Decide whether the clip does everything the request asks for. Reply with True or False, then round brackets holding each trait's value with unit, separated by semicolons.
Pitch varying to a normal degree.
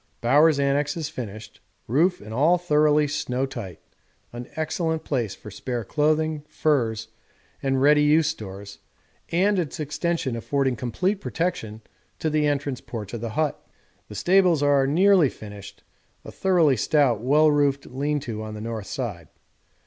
True (5.0 semitones)